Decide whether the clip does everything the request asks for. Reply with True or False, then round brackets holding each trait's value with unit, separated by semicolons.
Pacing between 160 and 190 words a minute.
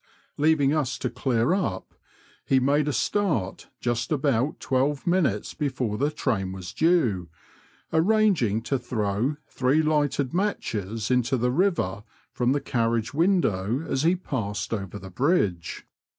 False (135 wpm)